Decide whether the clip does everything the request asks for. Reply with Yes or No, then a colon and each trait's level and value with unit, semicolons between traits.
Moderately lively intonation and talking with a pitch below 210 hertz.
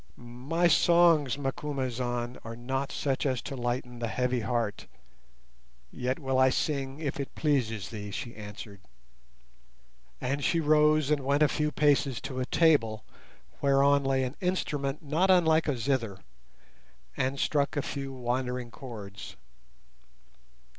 Yes: average, 3.3 semitones; low, 135 Hz